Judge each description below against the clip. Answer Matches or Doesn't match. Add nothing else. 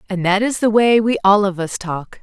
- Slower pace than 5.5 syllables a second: Matches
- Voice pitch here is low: Doesn't match